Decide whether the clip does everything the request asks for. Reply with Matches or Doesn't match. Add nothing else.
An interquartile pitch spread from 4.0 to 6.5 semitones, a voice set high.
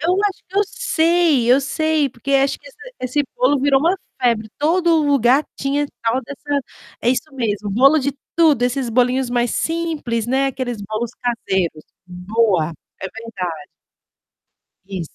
Matches